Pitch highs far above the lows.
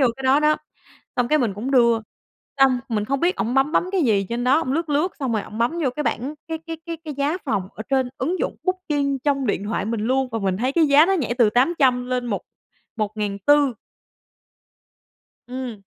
No: average, 4.3 semitones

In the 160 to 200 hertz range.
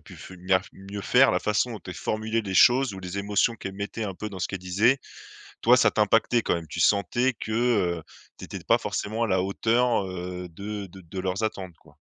No: low, 100 Hz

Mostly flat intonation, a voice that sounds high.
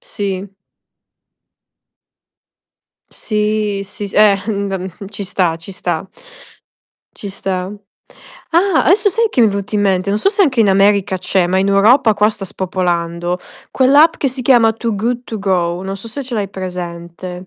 No: average, 3.3 semitones; high, 200 Hz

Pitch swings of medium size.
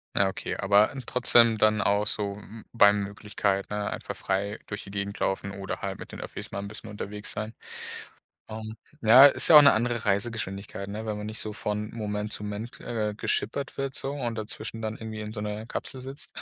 No: narrow, 1.6 semitones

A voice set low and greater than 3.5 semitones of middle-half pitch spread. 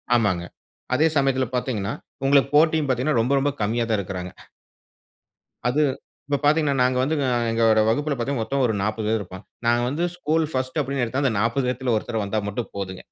Yes: low, 125 Hz; average, 4.1 semitones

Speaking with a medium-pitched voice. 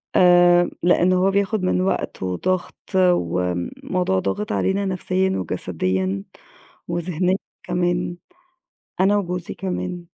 Yes: medium, 175 Hz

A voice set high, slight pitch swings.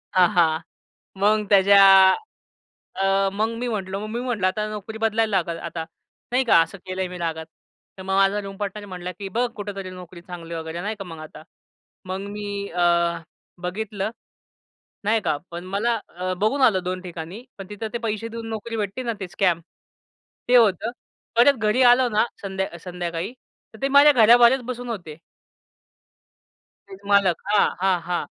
No: high, 195 Hz; average, 3.4 semitones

